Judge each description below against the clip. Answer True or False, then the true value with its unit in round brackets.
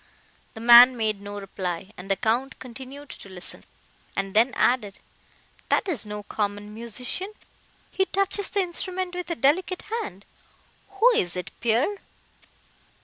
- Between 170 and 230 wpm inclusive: False (145 wpm)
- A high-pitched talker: True (235 Hz)